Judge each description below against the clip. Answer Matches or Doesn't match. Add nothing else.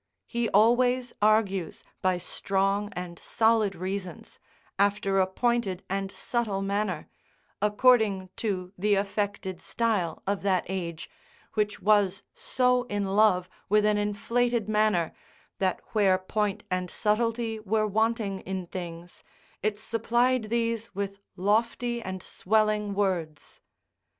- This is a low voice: Doesn't match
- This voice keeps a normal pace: Doesn't match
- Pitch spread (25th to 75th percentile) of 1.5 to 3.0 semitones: Matches